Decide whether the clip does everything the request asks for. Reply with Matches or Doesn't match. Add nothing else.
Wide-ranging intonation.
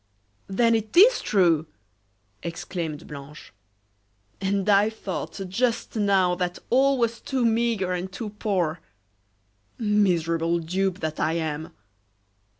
Doesn't match